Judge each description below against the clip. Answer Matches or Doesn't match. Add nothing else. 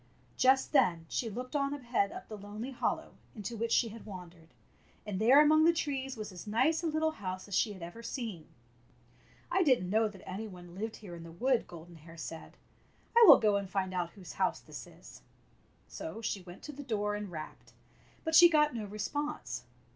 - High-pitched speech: Matches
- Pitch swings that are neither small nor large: Doesn't match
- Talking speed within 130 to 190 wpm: Doesn't match